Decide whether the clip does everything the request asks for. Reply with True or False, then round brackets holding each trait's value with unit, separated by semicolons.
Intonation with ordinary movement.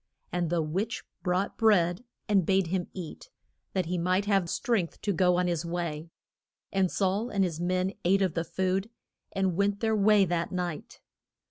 False (2.2 semitones)